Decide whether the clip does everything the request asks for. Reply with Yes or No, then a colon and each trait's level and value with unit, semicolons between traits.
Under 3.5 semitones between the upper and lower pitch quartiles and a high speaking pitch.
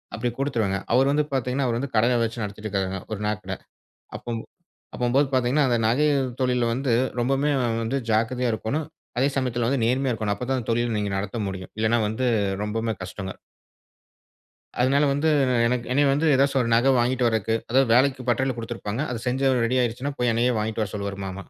No: average, 3.1 semitones; low, 120 Hz